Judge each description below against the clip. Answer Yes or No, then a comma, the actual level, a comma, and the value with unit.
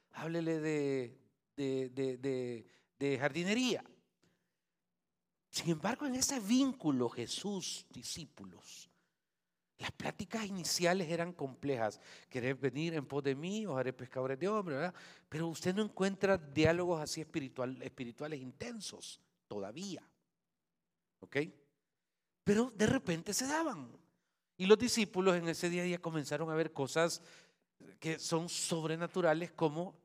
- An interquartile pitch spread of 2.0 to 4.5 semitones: No, wide, 5.4 semitones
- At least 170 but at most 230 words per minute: No, slow, 125 wpm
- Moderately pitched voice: Yes, medium, 165 Hz